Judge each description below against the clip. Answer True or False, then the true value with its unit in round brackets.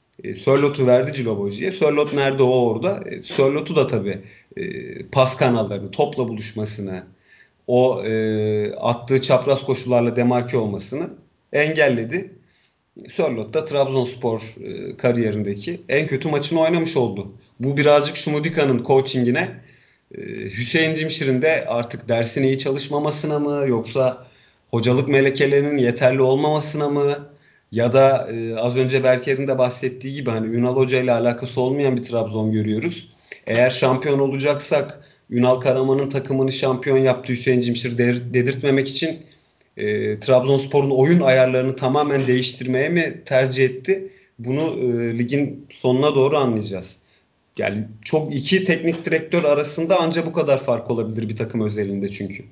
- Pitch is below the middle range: True (130 Hz)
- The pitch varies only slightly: False (3.2 semitones)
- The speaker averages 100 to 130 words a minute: True (125 wpm)